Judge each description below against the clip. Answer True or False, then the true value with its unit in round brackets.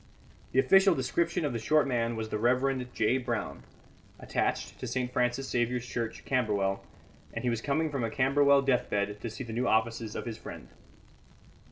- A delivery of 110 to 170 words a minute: False (180 wpm)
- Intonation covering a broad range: False (3.0 semitones)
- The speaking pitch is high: False (125 Hz)